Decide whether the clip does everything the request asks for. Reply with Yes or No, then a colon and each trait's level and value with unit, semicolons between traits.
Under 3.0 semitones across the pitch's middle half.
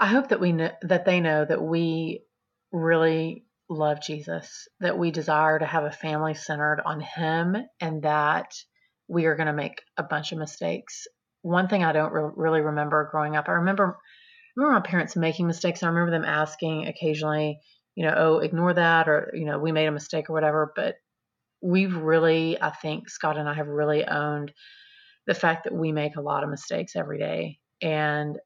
Yes: narrow, 2.5 semitones